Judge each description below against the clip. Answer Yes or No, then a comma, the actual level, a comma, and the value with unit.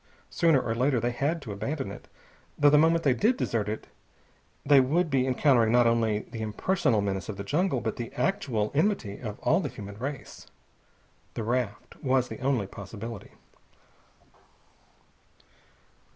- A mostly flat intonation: No, average, 5.0 semitones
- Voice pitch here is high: No, low, 125 Hz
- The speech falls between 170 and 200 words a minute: No, average, 155 wpm